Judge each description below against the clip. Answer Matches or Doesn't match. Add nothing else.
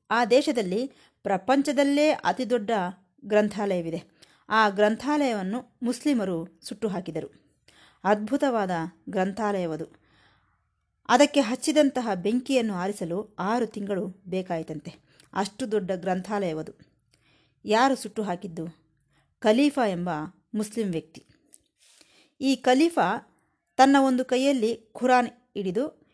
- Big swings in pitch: Matches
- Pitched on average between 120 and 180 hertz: Doesn't match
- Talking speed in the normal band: Matches